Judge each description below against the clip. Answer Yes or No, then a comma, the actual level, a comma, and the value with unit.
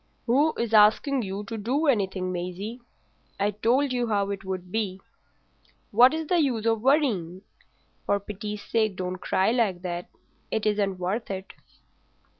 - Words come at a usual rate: Yes, average, 150 wpm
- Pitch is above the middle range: Yes, high, 210 Hz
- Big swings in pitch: No, average, 3.9 semitones